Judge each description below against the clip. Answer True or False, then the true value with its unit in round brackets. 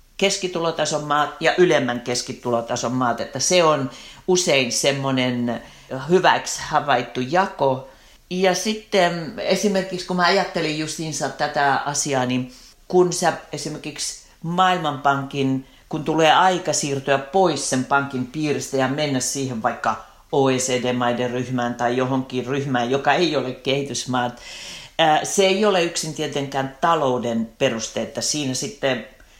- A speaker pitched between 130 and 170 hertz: True (140 Hz)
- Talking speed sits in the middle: True (120 wpm)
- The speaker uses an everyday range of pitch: True (4.5 semitones)